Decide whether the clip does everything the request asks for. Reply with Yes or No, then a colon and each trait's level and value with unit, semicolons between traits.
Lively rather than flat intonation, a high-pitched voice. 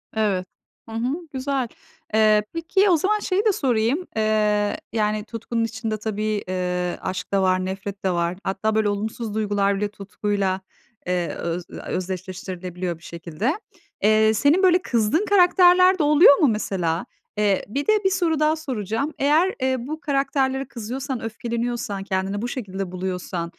Yes: wide, 6.3 semitones; high, 220 Hz